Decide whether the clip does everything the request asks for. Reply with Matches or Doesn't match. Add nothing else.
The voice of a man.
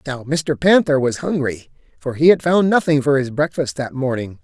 Matches